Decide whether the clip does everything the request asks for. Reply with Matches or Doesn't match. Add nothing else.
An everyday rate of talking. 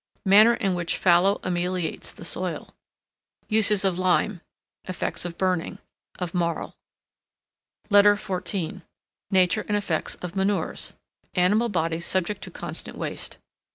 Doesn't match